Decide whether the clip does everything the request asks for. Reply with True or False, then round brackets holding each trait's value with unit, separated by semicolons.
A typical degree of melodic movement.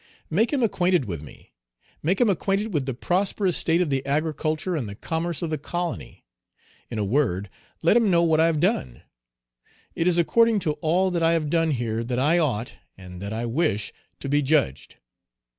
False (6.3 semitones)